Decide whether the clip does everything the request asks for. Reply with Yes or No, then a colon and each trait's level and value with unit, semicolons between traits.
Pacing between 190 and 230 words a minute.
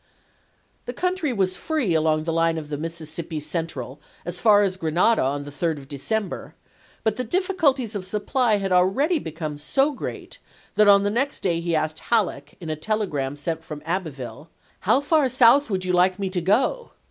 Yes: average, 200 wpm